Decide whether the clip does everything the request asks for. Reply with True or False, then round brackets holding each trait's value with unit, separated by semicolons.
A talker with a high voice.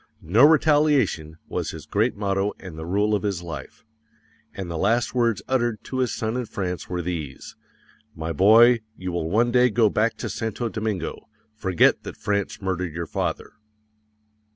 False (105 Hz)